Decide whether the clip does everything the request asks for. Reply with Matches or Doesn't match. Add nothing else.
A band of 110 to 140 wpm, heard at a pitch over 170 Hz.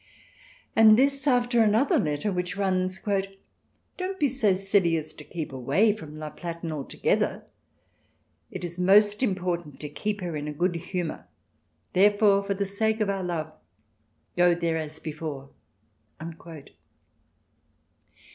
Matches